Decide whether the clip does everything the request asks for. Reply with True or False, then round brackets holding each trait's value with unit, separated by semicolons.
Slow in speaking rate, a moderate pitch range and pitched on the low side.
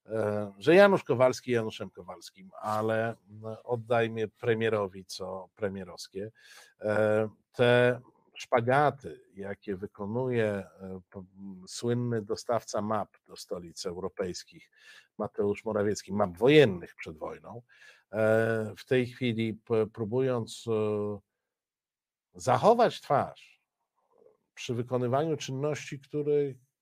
True (80 wpm; 3.2 semitones; 110 Hz)